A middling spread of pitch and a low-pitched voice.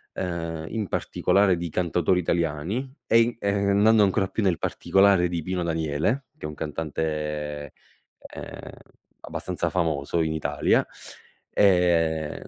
Yes: average, 3.8 semitones; very low, 85 Hz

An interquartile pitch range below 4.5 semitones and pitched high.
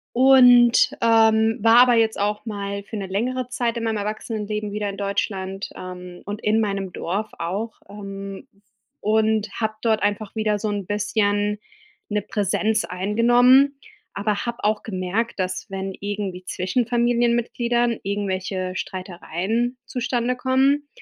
Yes: average, 2.9 semitones; high, 210 Hz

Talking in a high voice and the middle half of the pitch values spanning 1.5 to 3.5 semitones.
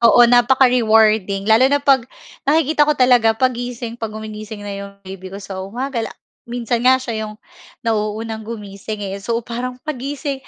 Yes: high, 230 Hz; average, 3.0 semitones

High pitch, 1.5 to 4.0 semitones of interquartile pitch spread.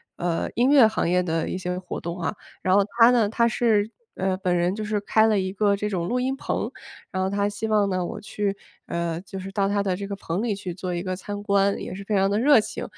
Yes: high, 200 Hz; narrow, 2.5 semitones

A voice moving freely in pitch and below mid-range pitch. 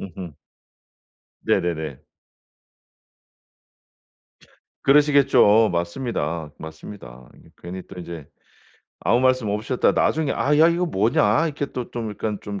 Yes: wide, 7.2 semitones; low, 105 Hz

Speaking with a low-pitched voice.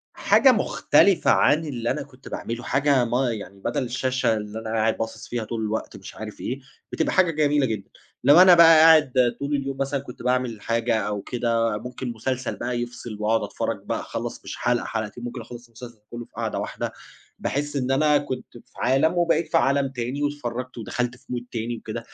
Yes: low, 125 Hz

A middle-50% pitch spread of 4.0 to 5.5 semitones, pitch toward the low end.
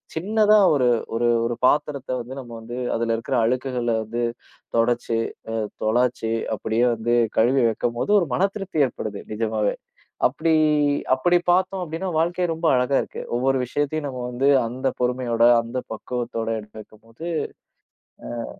Yes: average, 4.6 semitones; low, 125 Hz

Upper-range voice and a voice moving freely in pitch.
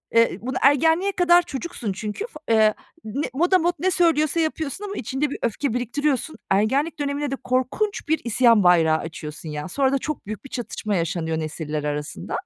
Yes: very high, 260 Hz; wide, 7.5 semitones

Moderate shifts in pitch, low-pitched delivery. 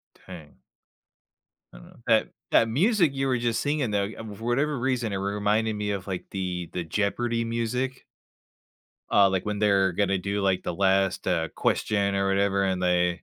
Yes: average, 3.5 semitones; low, 100 Hz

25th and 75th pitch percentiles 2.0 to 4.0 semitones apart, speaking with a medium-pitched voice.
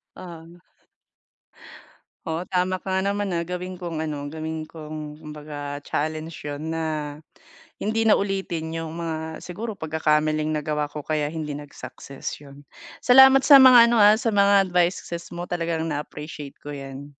Yes: average, 3.3 semitones; medium, 160 Hz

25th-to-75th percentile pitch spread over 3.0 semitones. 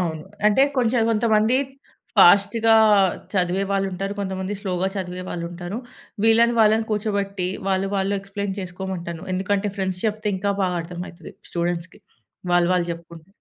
No: narrow, 2.6 semitones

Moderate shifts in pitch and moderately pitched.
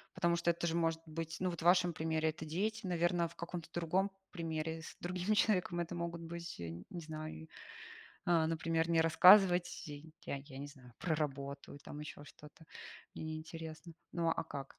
No: narrow, 1.7 semitones; medium, 165 Hz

